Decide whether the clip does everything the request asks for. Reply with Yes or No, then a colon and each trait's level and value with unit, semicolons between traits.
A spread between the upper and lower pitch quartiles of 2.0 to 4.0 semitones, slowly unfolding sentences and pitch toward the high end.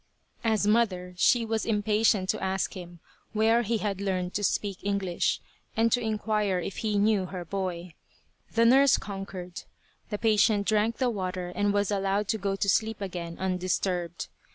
No: average, 2.9 semitones; average, 165 wpm; high, 200 Hz